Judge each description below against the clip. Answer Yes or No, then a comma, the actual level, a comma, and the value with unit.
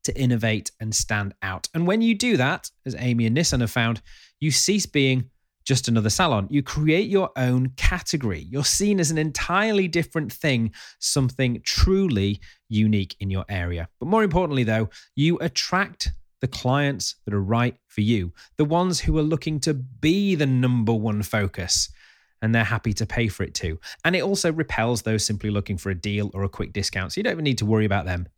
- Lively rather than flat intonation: Yes, wide, 6.7 semitones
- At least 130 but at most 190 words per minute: No, average, 200 wpm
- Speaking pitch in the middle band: No, low, 120 Hz